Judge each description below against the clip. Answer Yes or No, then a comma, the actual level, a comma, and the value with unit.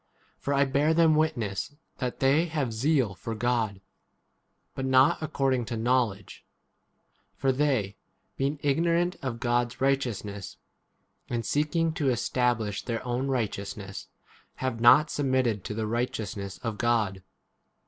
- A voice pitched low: Yes, low, 125 Hz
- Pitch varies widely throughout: No, average, 3.9 semitones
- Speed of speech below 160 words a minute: Yes, average, 140 wpm